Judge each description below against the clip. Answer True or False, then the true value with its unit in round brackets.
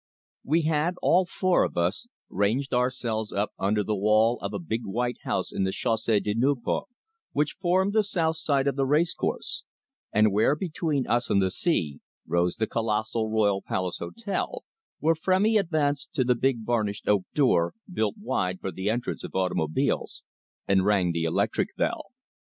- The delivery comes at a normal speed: True (170 wpm)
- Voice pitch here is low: True (115 Hz)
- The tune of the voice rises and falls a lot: True (7.0 semitones)